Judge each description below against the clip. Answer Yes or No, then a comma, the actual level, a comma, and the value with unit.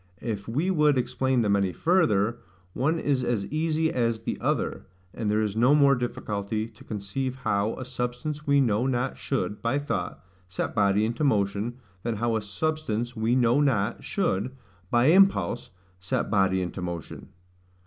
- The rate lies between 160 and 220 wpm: Yes, average, 165 wpm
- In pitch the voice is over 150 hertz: No, low, 120 Hz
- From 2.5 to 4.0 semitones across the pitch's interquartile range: No, average, 4.7 semitones